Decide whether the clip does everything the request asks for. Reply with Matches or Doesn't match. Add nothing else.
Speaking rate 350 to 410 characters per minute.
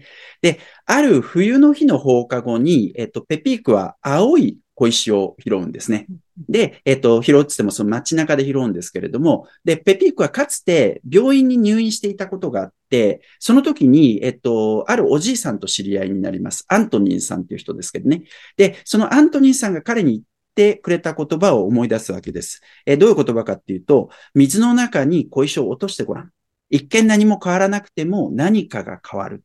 Matches